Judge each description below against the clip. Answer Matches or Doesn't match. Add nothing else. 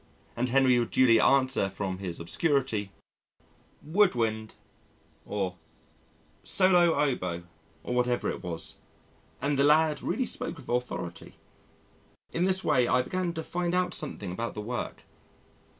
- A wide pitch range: Matches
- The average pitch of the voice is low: Matches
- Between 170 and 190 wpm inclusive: Doesn't match